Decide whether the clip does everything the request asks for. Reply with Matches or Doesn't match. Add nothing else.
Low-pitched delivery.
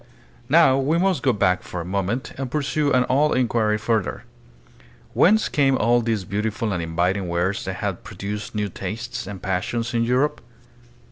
Matches